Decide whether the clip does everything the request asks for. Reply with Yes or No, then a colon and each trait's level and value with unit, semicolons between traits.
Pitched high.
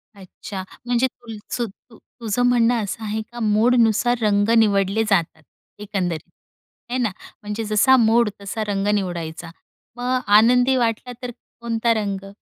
Yes: high, 220 Hz